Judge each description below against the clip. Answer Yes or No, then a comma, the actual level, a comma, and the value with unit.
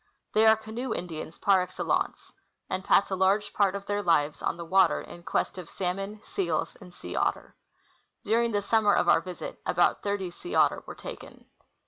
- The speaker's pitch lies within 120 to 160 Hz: No, high, 195 Hz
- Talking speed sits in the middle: Yes, average, 190 wpm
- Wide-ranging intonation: No, average, 2.7 semitones